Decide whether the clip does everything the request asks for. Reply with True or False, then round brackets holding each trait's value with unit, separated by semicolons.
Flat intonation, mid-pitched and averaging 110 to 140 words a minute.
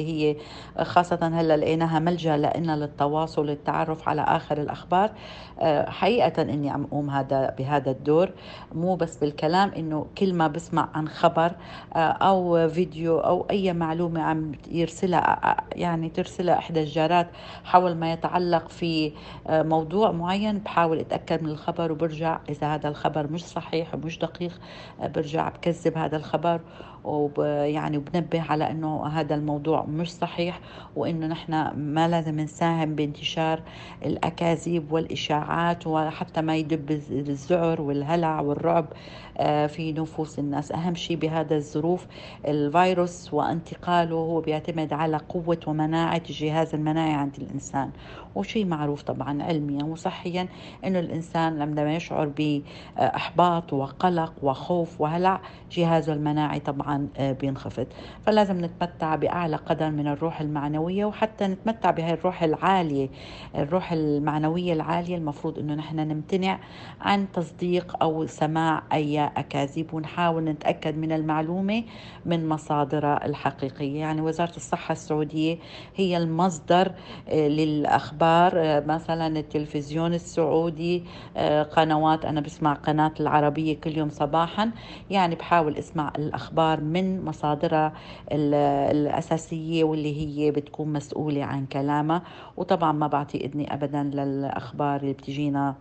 True (2.1 semitones; 160 Hz; 120 wpm)